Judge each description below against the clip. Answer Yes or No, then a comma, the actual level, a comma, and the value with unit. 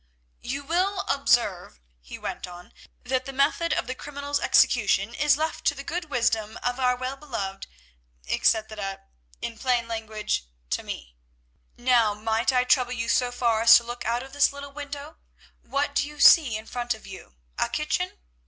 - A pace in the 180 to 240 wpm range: No, average, 170 wpm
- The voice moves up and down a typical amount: Yes, average, 4.4 semitones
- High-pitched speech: Yes, high, 245 Hz